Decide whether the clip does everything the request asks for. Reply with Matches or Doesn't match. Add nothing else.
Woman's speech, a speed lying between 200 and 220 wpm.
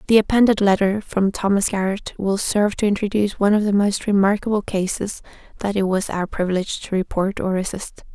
Doesn't match